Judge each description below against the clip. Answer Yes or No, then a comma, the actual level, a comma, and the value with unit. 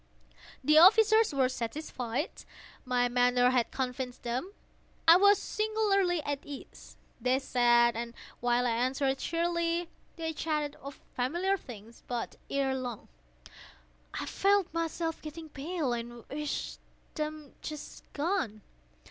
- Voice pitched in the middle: No, very high, 280 Hz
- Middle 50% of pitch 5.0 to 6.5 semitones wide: Yes, average, 5.3 semitones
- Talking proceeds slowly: Yes, slow, 120 wpm